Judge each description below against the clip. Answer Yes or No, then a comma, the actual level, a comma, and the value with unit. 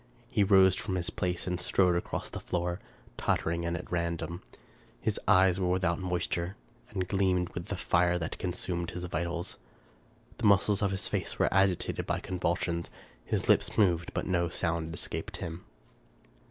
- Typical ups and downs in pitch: No, narrow, 1.6 semitones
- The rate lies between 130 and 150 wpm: No, average, 165 wpm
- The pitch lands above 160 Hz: No, very low, 90 Hz